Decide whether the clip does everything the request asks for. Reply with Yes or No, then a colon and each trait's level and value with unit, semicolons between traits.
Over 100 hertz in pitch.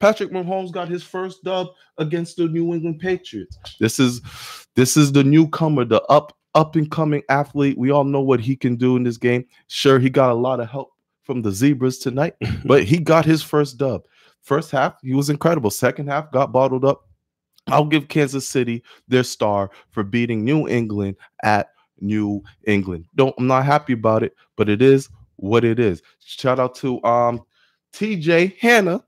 Yes: low, 135 Hz